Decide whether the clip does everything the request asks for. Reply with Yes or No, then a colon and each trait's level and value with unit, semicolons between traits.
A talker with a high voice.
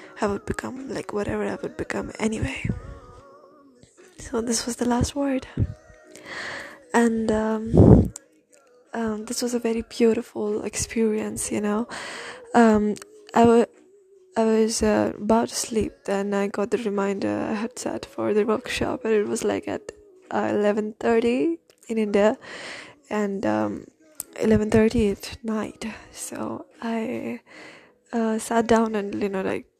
Yes: high, 225 Hz